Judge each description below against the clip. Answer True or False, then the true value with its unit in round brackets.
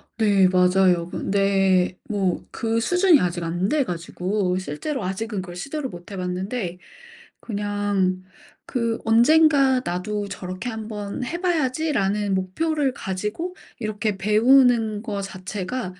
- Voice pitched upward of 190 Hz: True (205 Hz)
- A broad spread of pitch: False (5.0 semitones)